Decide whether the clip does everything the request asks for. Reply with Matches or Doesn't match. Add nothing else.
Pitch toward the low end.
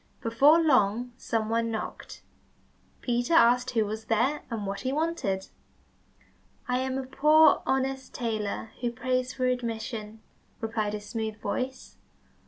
Doesn't match